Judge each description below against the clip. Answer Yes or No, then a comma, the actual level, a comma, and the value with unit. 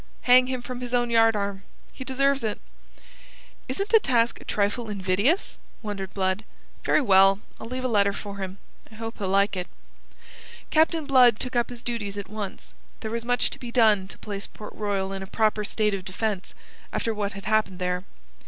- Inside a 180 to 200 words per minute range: Yes, average, 190 wpm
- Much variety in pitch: No, average, 3.6 semitones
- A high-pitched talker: Yes, high, 215 Hz